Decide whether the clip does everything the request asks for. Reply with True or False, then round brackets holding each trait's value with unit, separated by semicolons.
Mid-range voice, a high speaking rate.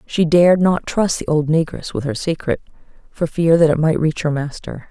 True (160 Hz; 220 wpm)